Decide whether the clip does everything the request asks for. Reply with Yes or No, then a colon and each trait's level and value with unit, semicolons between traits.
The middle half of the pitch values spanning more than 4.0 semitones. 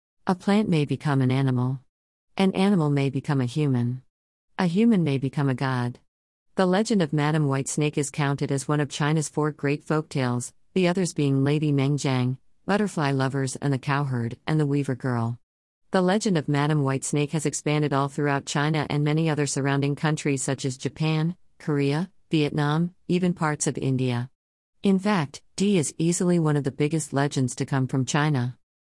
No: average, 2.7 semitones